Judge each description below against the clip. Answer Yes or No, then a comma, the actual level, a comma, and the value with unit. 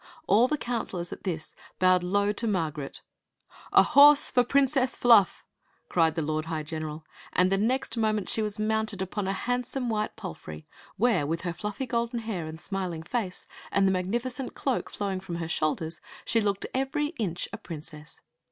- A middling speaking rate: Yes, average, 195 wpm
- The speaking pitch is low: No, high, 200 Hz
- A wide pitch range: Yes, wide, 5.7 semitones